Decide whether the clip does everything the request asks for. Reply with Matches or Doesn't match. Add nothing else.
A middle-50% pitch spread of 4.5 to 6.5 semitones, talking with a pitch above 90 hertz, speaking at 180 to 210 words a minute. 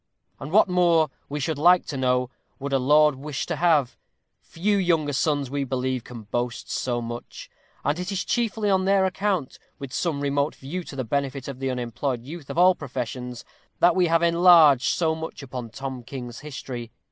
Matches